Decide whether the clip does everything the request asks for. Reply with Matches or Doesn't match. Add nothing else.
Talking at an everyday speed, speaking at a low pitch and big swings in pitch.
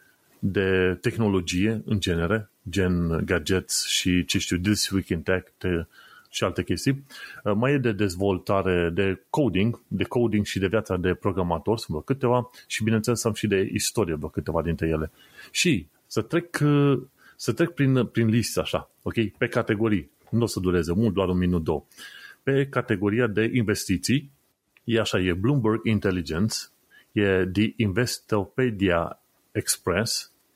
Doesn't match